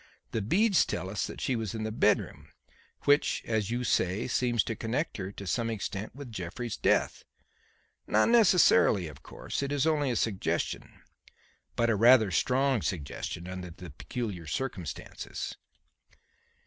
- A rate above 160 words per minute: No, average, 150 wpm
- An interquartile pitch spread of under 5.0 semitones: No, wide, 5.4 semitones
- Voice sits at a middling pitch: No, low, 110 Hz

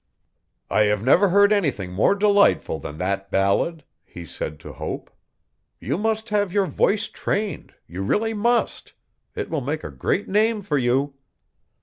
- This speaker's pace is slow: No, average, 155 wpm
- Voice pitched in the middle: Yes, medium, 170 Hz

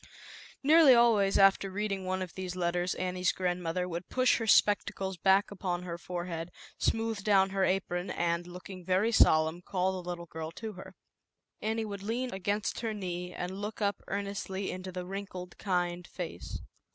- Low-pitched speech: No, high, 190 Hz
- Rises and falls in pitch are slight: Yes, narrow, 2.2 semitones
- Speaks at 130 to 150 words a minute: No, average, 175 wpm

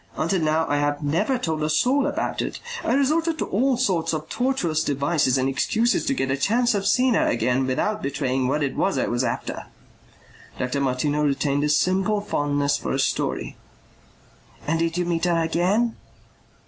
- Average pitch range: No, wide, 7.0 semitones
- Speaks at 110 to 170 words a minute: No, average, 185 wpm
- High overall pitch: No, medium, 160 Hz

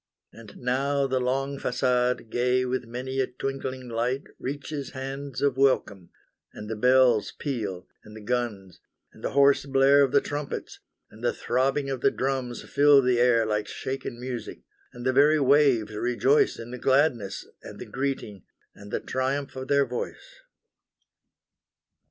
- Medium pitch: No, low, 130 Hz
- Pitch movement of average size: No, narrow, 2.3 semitones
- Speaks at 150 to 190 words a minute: Yes, average, 155 wpm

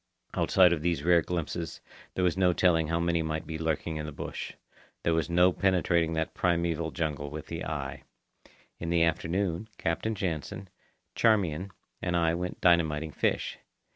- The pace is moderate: Yes, average, 165 wpm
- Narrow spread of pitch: Yes, narrow, 1.9 semitones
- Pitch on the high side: No, very low, 85 Hz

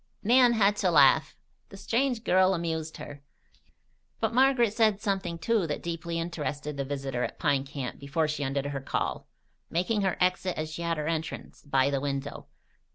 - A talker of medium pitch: Yes, medium, 165 Hz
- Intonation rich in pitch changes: Yes, wide, 5.7 semitones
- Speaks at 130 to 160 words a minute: No, average, 175 wpm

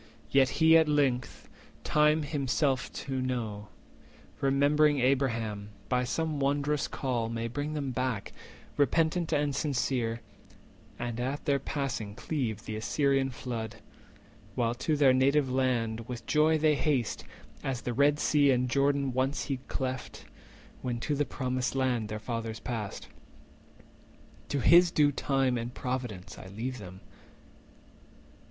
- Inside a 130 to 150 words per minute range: Yes, slow, 135 wpm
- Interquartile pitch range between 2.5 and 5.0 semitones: Yes, average, 3.3 semitones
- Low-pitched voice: Yes, low, 130 Hz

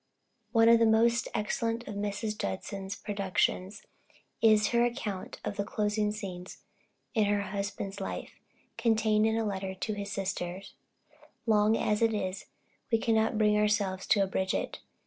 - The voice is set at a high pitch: Yes, high, 210 Hz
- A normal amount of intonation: No, narrow, 2.0 semitones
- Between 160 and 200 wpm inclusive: No, average, 150 wpm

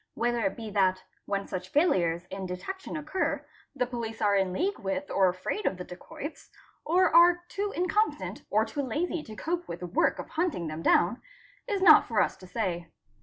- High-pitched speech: Yes, high, 225 Hz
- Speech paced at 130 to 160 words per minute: No, average, 195 wpm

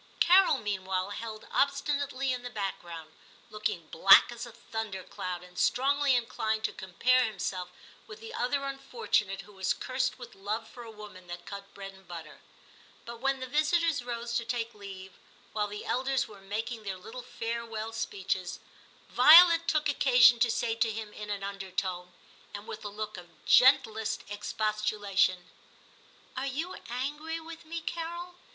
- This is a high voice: Yes, high, 225 Hz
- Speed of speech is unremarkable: Yes, average, 165 wpm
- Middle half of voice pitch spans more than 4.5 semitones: Yes, average, 4.9 semitones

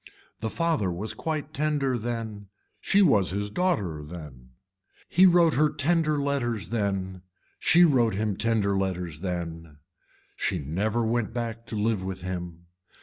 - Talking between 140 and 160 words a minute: Yes, average, 145 wpm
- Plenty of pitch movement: Yes, wide, 7.4 semitones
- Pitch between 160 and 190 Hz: No, low, 110 Hz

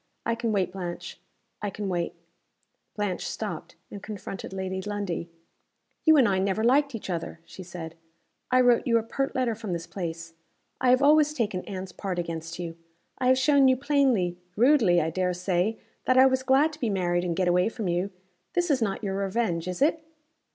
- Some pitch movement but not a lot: No, wide, 6.1 semitones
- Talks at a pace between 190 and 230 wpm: Yes, average, 195 wpm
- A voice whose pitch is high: Yes, high, 200 Hz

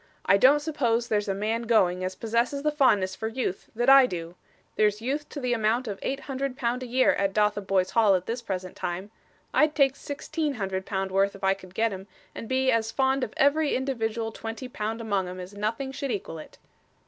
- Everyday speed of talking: No, fast, 215 wpm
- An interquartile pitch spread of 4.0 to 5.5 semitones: Yes, average, 5.0 semitones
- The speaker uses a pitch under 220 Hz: No, high, 225 Hz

